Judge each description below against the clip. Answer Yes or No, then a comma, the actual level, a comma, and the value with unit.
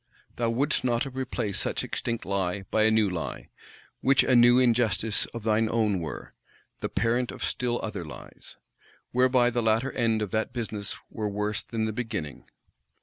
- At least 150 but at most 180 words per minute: Yes, average, 170 wpm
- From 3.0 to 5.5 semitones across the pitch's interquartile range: No, narrow, 2.4 semitones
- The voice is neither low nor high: No, low, 115 Hz